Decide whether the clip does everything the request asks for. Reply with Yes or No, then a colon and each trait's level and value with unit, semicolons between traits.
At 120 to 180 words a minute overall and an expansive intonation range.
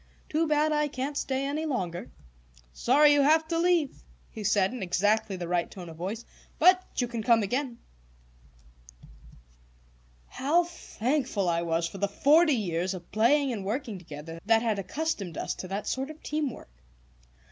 Yes: average, 170 wpm; wide, 7.6 semitones